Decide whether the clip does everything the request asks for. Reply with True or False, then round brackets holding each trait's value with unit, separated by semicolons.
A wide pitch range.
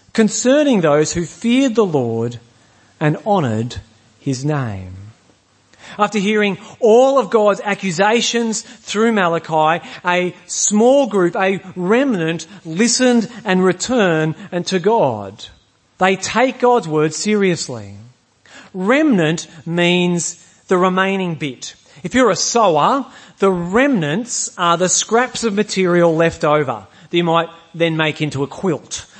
True (6.0 semitones)